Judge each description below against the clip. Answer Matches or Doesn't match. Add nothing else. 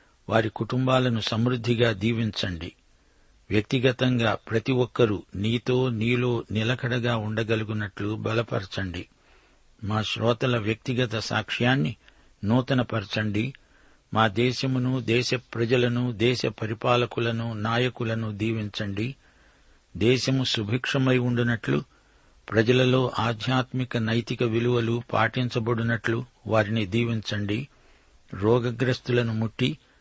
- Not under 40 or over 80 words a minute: Matches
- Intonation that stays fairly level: Matches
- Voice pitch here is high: Doesn't match